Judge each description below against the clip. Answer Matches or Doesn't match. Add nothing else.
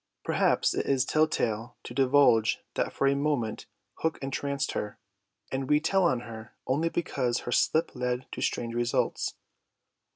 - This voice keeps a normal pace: Matches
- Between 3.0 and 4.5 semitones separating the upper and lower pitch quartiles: Matches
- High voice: Doesn't match